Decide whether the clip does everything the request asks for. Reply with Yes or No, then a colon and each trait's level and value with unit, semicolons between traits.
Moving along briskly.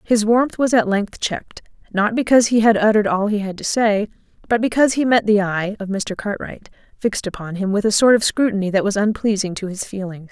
Yes: fast, 225 wpm